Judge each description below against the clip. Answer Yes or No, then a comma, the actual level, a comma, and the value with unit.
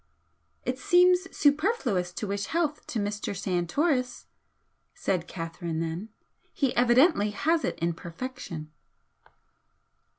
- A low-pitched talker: No, high, 220 Hz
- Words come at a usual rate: No, slow, 105 wpm